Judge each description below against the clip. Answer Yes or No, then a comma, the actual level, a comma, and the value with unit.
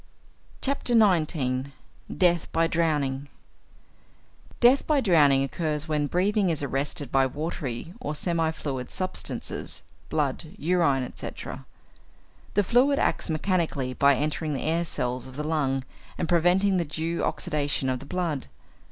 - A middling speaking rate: No, slow, 130 wpm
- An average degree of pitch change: Yes, average, 4.3 semitones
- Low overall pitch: No, medium, 155 Hz